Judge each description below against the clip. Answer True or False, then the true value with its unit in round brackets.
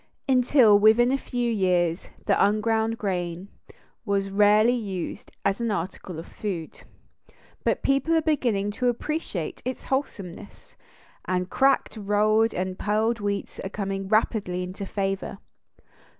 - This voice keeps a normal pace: False (130 wpm)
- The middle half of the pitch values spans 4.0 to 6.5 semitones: False (3.4 semitones)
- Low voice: False (205 Hz)